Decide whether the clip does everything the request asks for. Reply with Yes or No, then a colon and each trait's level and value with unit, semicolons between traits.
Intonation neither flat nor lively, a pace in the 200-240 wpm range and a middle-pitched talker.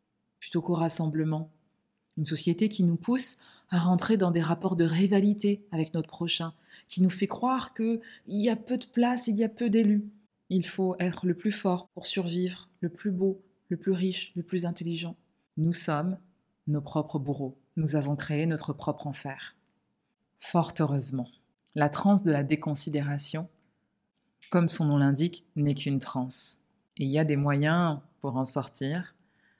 No: average, 4.1 semitones; average, 170 wpm; medium, 170 Hz